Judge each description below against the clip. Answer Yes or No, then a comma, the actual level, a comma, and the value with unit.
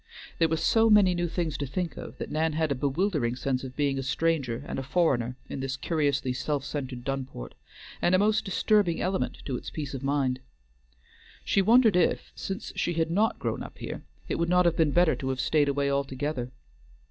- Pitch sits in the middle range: Yes, medium, 150 Hz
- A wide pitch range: No, average, 4.6 semitones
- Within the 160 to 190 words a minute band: No, fast, 205 wpm